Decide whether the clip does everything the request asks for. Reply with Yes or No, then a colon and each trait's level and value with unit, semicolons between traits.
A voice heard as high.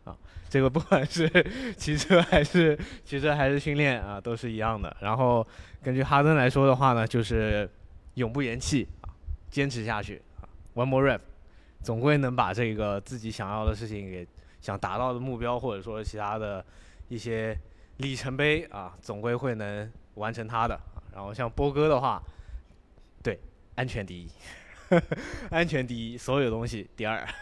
No: low, 115 Hz